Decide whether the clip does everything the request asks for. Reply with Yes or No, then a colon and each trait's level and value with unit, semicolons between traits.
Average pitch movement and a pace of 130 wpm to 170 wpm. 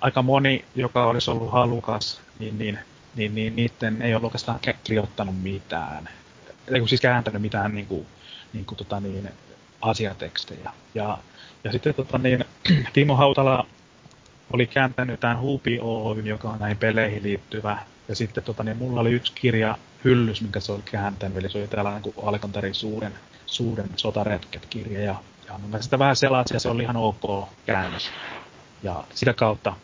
Yes: average, 3.1 semitones; average, 150 wpm